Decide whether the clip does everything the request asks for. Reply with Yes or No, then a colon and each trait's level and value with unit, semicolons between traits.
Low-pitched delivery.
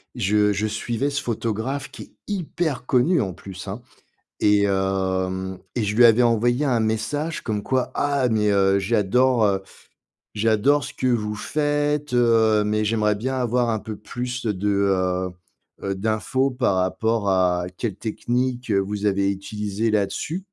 Yes: low, 110 Hz